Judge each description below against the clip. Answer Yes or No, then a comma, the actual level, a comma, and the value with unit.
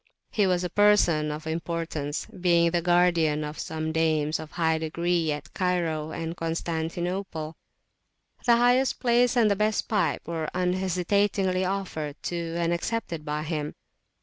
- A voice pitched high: No, medium, 170 Hz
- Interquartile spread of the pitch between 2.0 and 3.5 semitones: Yes, average, 2.8 semitones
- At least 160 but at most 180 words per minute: No, average, 150 wpm